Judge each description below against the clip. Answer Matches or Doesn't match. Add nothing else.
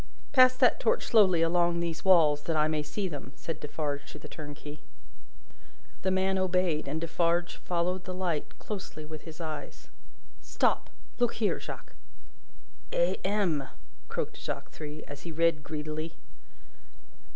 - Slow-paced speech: Doesn't match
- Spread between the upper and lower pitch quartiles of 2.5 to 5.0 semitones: Matches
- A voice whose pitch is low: Doesn't match